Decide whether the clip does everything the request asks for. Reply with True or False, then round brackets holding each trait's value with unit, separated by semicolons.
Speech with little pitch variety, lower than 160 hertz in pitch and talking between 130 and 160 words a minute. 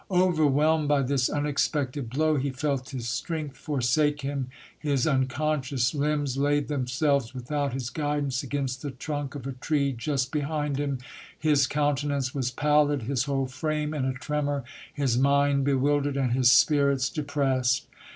True (2.1 semitones; 140 Hz; 150 wpm)